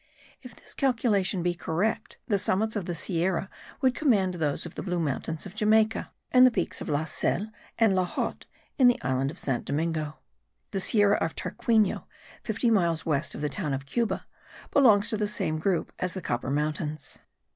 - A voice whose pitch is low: No, medium, 185 Hz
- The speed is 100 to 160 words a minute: No, average, 190 wpm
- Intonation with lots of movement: Yes, wide, 5.7 semitones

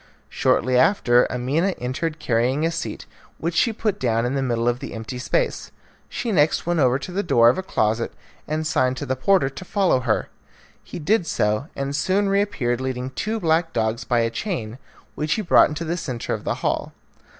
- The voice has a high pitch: No, medium, 140 Hz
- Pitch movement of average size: No, wide, 6.1 semitones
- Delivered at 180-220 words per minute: Yes, average, 200 wpm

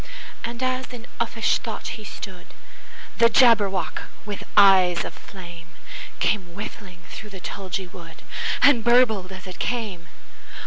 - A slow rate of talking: Yes, slow, 120 wpm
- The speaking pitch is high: Yes, high, 200 Hz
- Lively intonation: No, average, 4.2 semitones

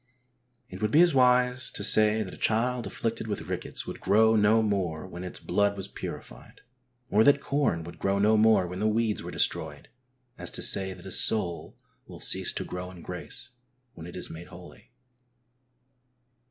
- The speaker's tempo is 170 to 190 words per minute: Yes, average, 185 wpm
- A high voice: No, low, 105 Hz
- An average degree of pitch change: Yes, average, 3.5 semitones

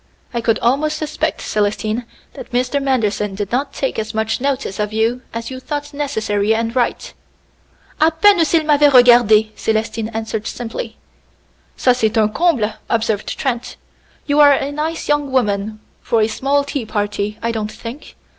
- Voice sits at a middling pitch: No, high, 235 Hz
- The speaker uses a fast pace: No, average, 165 wpm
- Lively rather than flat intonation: No, average, 4.5 semitones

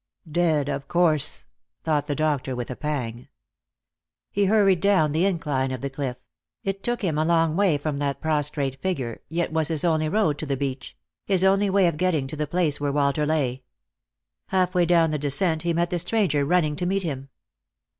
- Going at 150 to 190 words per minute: No, average, 200 wpm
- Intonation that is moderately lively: Yes, average, 3.9 semitones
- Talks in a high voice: No, medium, 155 Hz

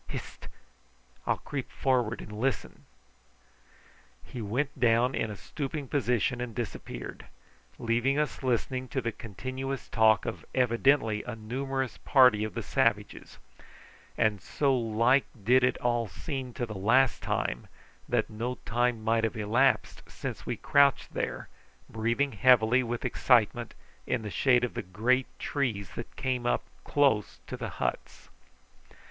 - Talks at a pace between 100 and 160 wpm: Yes, average, 140 wpm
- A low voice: Yes, low, 120 Hz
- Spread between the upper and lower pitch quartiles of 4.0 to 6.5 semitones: No, average, 2.9 semitones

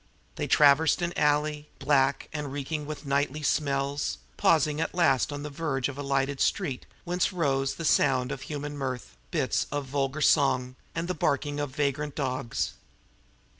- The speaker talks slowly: No, average, 165 wpm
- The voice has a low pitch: No, medium, 145 Hz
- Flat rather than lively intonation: Yes, narrow, 1.9 semitones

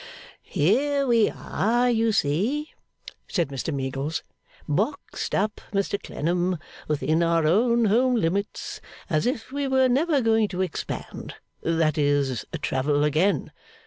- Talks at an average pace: No, slow, 125 wpm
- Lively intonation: Yes, wide, 7.6 semitones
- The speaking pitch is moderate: No, high, 195 Hz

